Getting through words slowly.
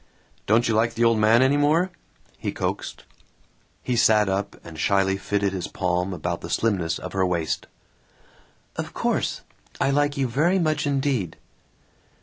No: average, 155 wpm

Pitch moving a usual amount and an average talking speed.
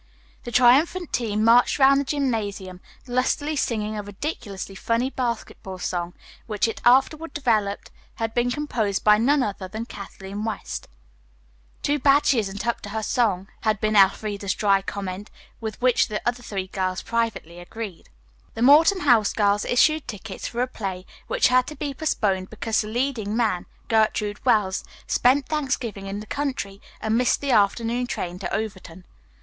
Yes: average, 4.0 semitones; average, 165 wpm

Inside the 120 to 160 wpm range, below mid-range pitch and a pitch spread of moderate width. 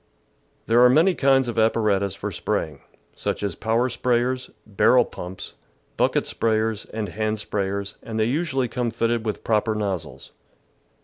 Yes: average, 150 wpm; low, 110 Hz; average, 3.3 semitones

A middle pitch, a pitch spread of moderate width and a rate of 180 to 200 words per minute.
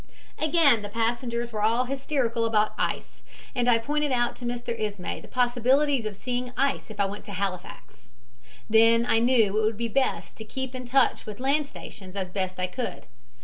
No: high, 235 Hz; average, 3.2 semitones; average, 190 wpm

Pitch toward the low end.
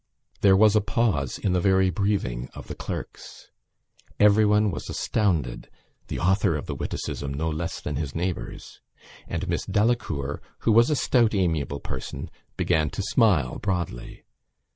Yes: very low, 95 Hz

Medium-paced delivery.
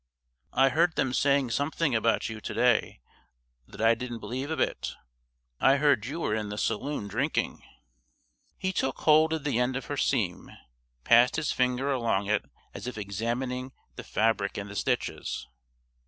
Yes: average, 170 wpm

